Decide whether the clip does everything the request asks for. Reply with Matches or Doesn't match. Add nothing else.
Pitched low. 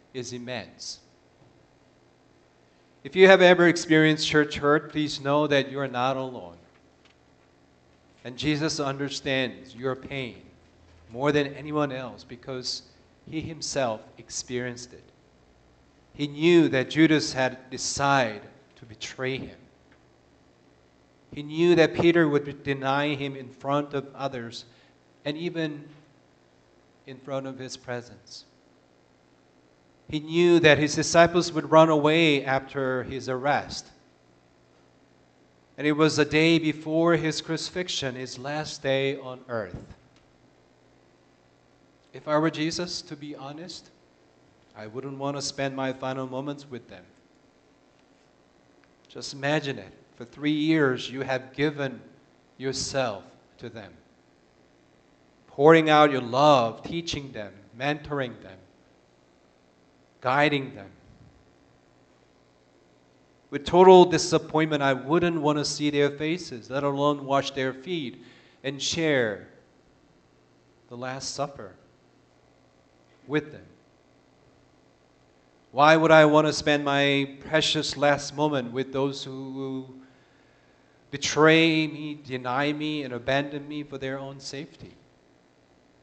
Matches